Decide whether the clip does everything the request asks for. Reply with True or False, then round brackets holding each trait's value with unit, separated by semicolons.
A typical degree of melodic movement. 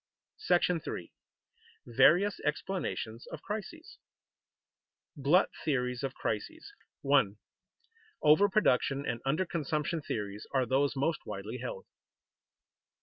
False (6.1 semitones)